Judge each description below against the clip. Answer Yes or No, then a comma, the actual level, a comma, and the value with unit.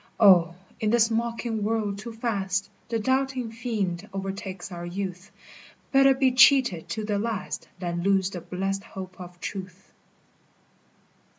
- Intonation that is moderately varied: Yes, average, 3.6 semitones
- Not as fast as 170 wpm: Yes, slow, 135 wpm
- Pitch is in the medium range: No, high, 200 Hz